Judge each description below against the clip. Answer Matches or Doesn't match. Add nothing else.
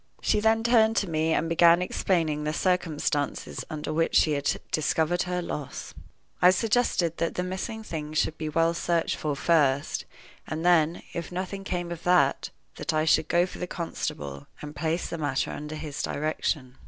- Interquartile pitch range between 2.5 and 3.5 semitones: Matches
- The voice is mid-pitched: Matches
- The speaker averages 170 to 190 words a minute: Matches